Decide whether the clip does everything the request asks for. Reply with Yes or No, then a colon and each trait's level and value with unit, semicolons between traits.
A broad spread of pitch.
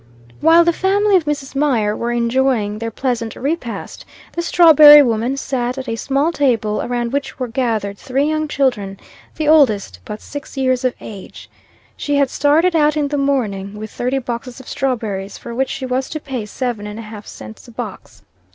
No: average, 4.2 semitones